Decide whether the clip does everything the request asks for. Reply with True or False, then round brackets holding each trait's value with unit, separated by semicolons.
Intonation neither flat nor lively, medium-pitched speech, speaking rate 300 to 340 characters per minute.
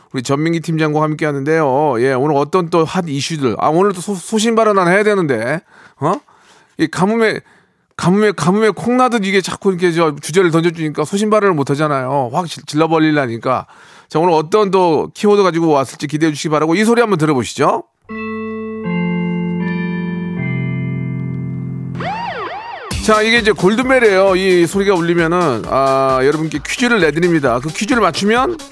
True (5.0 semitones; 175 Hz; 325 characters per minute)